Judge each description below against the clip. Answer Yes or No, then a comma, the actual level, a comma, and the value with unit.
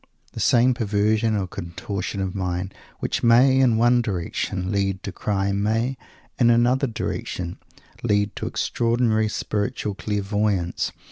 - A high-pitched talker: No, low, 105 Hz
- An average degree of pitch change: Yes, average, 3.2 semitones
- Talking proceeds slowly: Yes, slow, 130 wpm